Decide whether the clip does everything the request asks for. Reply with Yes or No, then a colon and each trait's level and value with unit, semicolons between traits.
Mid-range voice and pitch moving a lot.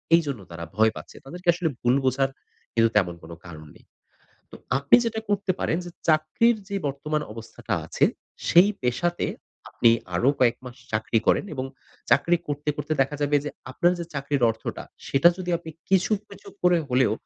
Yes: medium, 145 Hz; wide, 6.1 semitones